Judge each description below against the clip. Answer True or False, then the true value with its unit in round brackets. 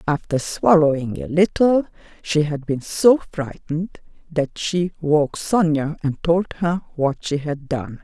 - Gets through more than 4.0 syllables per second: False (3.9 syllables/s)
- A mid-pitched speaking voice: True (160 Hz)